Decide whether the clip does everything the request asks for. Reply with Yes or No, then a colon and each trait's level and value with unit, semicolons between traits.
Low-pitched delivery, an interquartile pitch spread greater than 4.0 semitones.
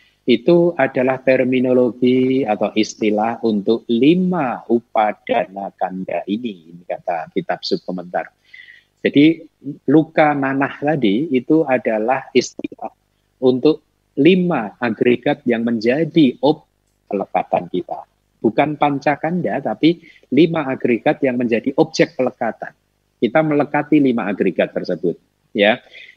Yes: low, 130 Hz; average, 4.7 semitones